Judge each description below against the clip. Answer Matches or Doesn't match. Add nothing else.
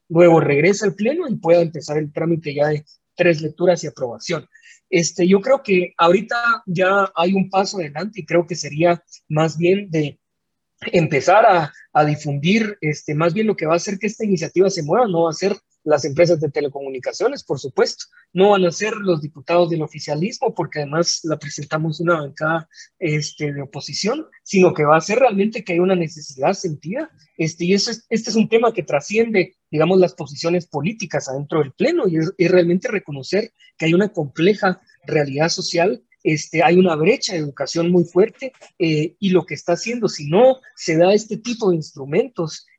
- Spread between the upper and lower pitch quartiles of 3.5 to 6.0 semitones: Matches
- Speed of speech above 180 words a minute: Matches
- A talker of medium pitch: Matches